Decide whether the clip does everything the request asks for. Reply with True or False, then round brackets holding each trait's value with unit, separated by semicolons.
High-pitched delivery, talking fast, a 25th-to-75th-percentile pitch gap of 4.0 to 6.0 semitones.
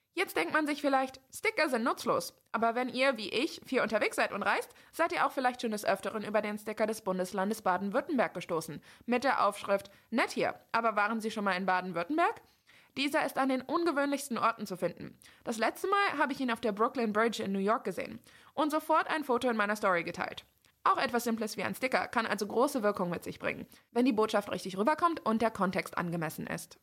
True (230 Hz; 215 wpm; 5.1 semitones)